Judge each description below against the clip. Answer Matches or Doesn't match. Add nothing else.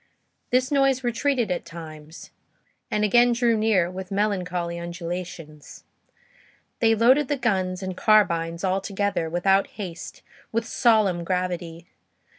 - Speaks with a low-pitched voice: Doesn't match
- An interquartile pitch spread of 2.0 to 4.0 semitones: Doesn't match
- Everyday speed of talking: Doesn't match